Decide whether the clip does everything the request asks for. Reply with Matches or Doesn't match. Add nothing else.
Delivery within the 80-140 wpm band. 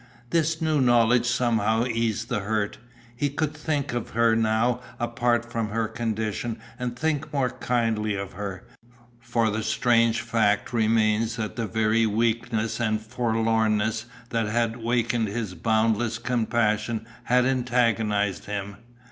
Matches